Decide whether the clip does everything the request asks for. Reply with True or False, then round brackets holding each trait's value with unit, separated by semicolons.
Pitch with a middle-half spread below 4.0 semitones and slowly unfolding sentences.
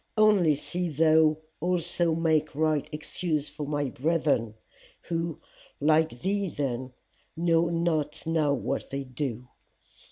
True (2.6 semitones; 120 wpm)